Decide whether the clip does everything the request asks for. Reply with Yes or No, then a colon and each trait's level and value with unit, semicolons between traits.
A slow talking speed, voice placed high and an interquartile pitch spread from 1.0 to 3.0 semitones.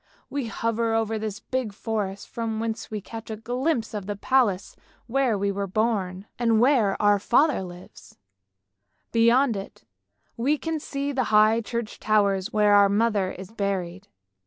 No: average, 160 wpm; high, 220 Hz; average, 2.7 semitones